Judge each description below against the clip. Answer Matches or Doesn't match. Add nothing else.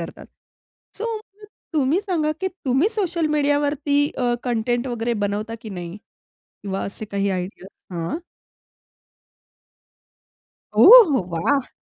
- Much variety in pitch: Matches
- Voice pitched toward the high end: Matches